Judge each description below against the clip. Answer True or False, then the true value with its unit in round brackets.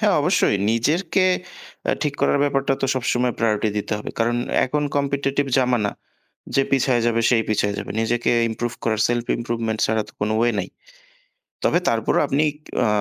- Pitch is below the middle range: True (120 Hz)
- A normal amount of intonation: True (3.5 semitones)